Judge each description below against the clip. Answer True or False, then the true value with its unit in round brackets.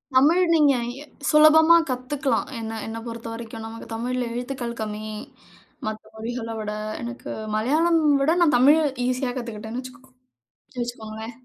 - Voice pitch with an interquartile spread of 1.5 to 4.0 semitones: True (3.6 semitones)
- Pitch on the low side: False (245 Hz)